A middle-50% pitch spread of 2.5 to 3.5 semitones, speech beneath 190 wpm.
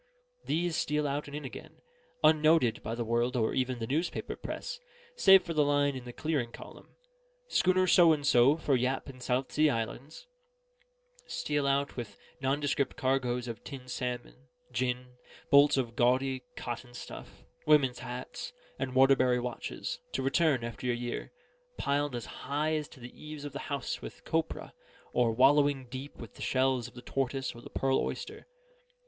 Yes: average, 2.8 semitones; average, 170 wpm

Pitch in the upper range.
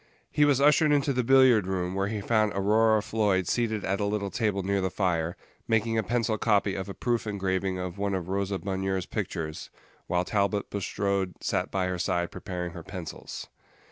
No: low, 100 Hz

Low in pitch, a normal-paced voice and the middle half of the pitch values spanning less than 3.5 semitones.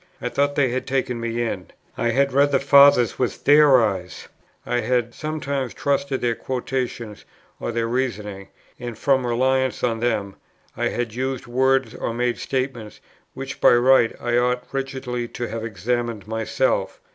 Yes: low, 125 Hz; average, 160 wpm; narrow, 2.4 semitones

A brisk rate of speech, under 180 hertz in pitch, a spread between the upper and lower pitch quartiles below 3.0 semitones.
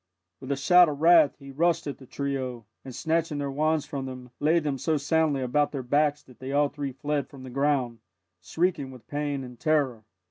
Yes: fast, 210 wpm; medium, 140 Hz; narrow, 2.5 semitones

